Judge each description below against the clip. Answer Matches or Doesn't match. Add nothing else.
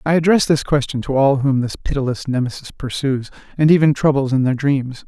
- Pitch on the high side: Doesn't match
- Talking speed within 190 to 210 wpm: Matches